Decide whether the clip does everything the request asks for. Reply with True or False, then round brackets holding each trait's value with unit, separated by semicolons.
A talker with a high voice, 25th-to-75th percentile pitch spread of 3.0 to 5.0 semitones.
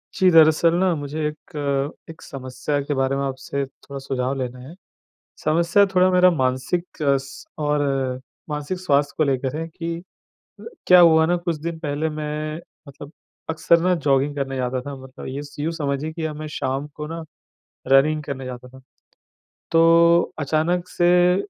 False (150 Hz; 3.4 semitones)